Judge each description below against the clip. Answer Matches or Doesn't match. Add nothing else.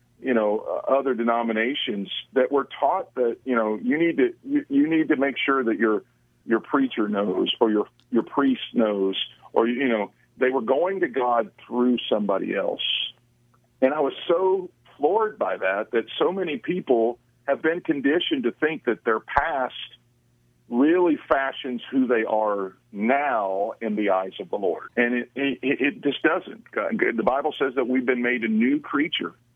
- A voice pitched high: Doesn't match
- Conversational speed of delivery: Matches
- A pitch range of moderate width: Doesn't match